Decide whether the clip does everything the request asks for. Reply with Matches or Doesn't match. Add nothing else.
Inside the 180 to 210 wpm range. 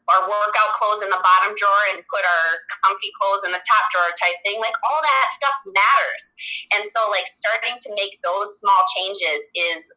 Matches